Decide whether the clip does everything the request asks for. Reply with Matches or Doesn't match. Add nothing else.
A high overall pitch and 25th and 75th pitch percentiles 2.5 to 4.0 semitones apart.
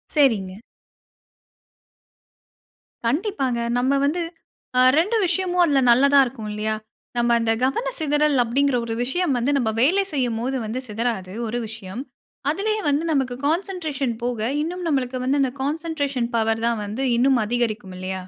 Doesn't match